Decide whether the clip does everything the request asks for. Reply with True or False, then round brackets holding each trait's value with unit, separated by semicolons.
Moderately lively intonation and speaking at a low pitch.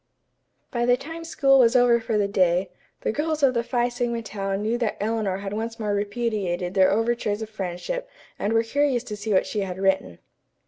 False (3.6 semitones; 220 Hz)